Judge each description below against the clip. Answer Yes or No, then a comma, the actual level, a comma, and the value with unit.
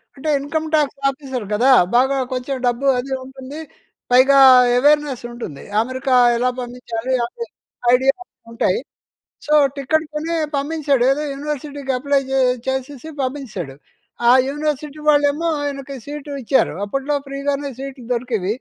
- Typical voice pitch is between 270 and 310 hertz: Yes, very high, 275 Hz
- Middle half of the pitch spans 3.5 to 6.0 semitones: No, narrow, 2.4 semitones